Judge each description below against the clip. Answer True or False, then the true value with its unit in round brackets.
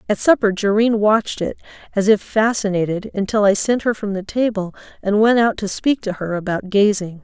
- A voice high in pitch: True (205 Hz)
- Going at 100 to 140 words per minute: False (200 wpm)